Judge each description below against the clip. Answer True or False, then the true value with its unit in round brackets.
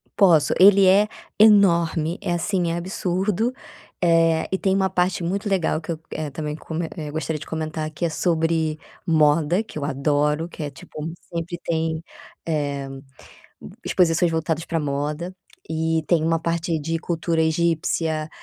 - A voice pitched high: False (165 Hz)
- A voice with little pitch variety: True (2.0 semitones)